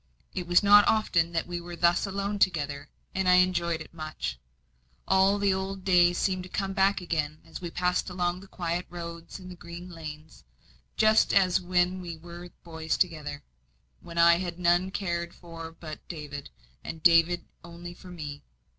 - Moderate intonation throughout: No, narrow, 1.8 semitones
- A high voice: No, medium, 175 Hz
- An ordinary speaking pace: Yes, average, 180 wpm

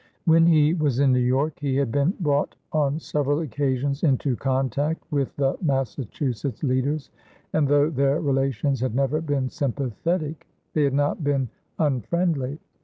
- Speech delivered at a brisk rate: No, average, 150 wpm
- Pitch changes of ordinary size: No, narrow, 2.2 semitones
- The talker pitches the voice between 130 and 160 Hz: Yes, medium, 140 Hz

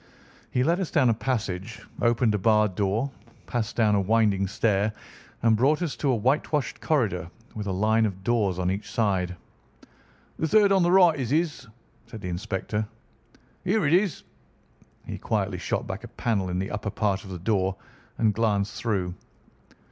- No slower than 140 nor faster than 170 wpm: No, average, 180 wpm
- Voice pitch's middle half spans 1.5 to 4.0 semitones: No, average, 4.6 semitones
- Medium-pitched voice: No, low, 110 Hz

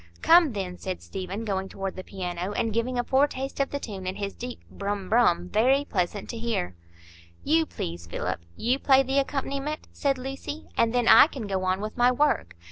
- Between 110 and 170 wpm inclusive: No, average, 195 wpm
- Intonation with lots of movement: Yes, wide, 6.1 semitones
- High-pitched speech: Yes, high, 225 Hz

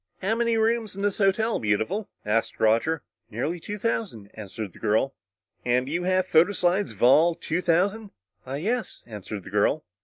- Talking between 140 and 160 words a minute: No, average, 175 wpm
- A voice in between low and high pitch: Yes, medium, 170 Hz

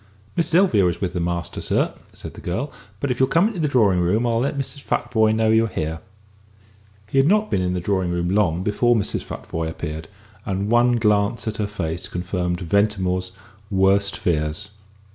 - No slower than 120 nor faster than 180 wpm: No, average, 195 wpm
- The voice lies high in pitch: No, low, 100 Hz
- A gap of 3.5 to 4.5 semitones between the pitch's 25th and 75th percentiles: No, average, 5.0 semitones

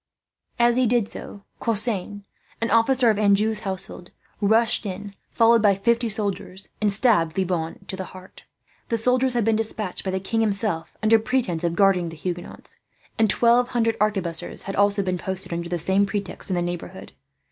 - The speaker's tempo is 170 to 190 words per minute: Yes, average, 180 wpm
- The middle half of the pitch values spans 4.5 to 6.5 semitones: No, average, 3.4 semitones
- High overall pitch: Yes, high, 205 Hz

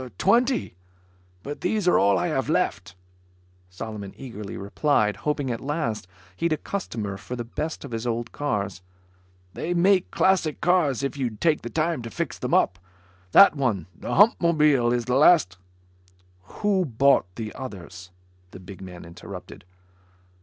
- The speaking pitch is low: Yes, low, 125 Hz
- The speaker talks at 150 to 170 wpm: Yes, average, 155 wpm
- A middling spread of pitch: No, wide, 8.0 semitones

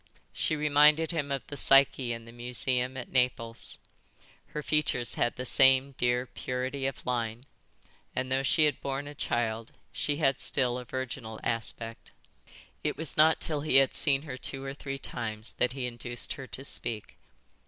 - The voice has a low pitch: Yes, low, 130 Hz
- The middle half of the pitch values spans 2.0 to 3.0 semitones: Yes, narrow, 2.5 semitones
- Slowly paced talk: No, average, 175 wpm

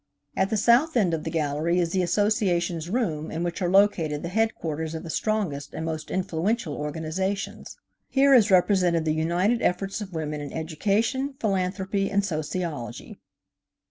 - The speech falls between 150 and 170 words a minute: Yes, average, 160 wpm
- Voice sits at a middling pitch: Yes, medium, 180 Hz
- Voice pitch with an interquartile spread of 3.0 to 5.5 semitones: Yes, average, 4.3 semitones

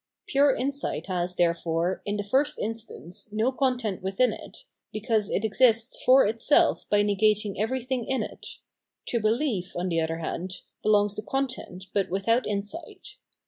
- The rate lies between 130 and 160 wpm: Yes, average, 150 wpm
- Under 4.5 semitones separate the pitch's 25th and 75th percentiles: No, average, 4.8 semitones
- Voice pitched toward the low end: No, high, 215 Hz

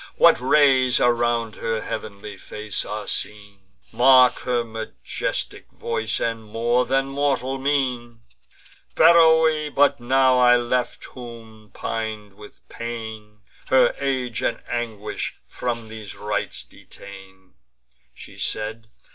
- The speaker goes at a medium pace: No, slow, 115 wpm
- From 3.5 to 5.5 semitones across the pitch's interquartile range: No, average, 3.0 semitones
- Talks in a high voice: No, low, 115 Hz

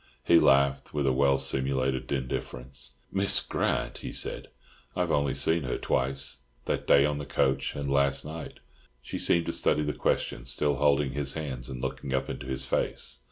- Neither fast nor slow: Yes, average, 180 wpm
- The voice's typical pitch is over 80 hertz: No, very low, 70 Hz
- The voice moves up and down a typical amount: No, narrow, 1.6 semitones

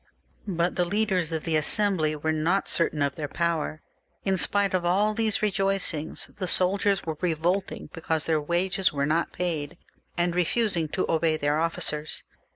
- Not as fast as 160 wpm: No, average, 165 wpm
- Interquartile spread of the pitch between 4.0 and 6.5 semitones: No, average, 3.6 semitones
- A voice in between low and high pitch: Yes, medium, 170 Hz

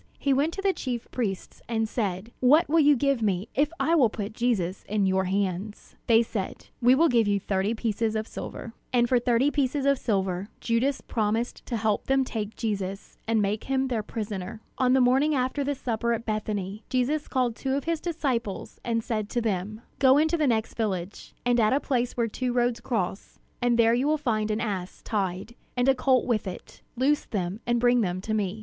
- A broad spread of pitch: No, average, 3.8 semitones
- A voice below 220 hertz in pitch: No, high, 230 Hz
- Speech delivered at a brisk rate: Yes, fast, 210 wpm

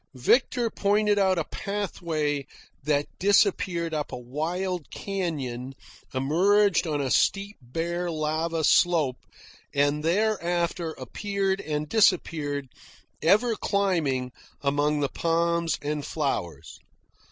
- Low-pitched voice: No, medium, 165 Hz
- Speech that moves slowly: Yes, slow, 105 wpm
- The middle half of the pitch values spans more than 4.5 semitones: Yes, average, 4.9 semitones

